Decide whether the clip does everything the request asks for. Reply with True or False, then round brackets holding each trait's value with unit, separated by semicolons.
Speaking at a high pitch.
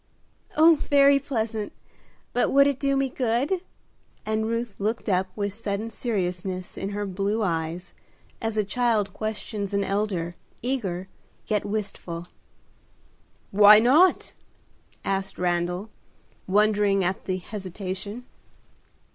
True (210 Hz)